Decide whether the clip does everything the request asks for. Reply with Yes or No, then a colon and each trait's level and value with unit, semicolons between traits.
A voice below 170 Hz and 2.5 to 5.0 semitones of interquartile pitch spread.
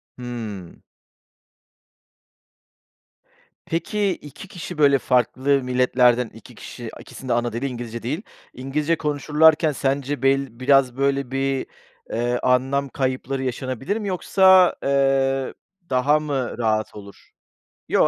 Yes: low, 135 Hz; average, 2.8 semitones